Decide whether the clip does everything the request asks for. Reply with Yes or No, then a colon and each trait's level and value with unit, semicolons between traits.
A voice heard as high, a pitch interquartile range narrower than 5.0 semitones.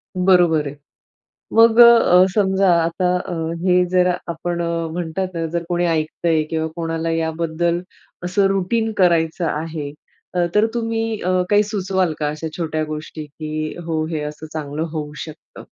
No: medium, 170 Hz; average, 2.9 semitones